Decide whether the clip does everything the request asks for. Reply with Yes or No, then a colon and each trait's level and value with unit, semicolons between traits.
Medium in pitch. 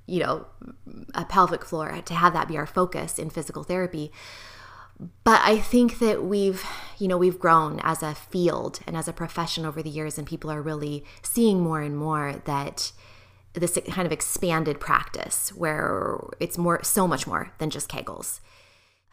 Yes: medium, 160 Hz